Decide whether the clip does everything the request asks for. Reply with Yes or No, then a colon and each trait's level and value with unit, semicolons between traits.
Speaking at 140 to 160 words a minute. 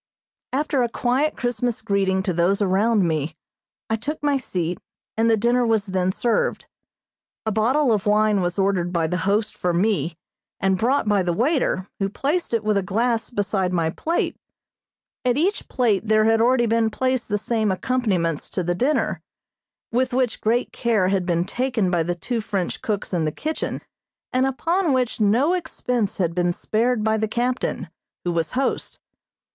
No: average, 175 wpm